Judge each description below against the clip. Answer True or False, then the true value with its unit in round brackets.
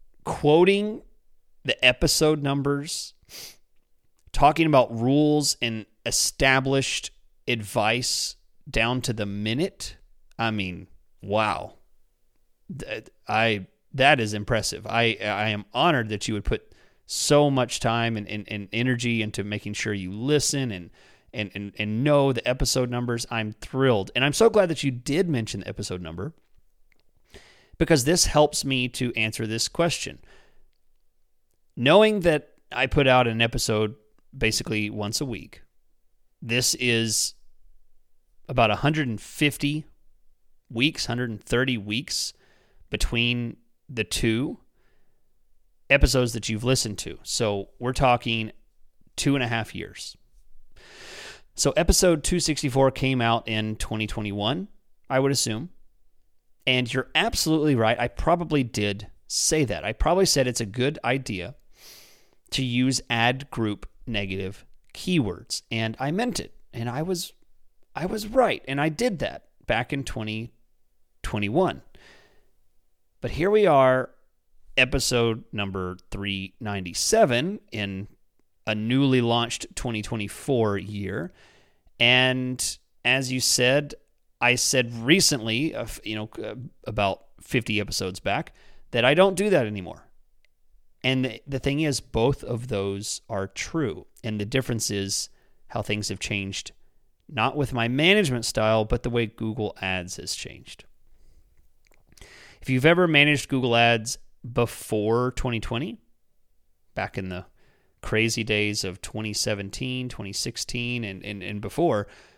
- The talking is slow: True (130 wpm)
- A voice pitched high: False (115 Hz)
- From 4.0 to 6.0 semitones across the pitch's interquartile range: True (4.5 semitones)